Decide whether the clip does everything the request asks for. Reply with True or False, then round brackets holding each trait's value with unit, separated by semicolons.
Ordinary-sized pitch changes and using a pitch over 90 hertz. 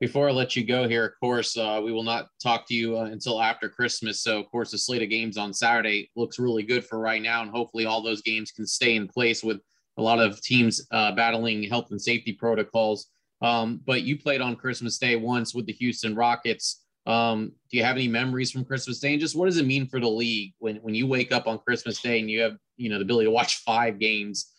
False (1.8 semitones; 115 Hz)